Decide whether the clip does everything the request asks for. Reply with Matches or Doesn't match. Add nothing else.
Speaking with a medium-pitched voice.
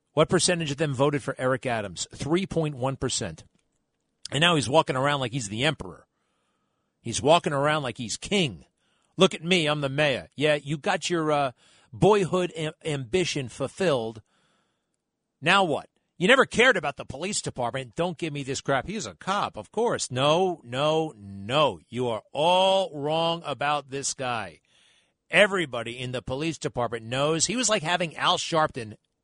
Matches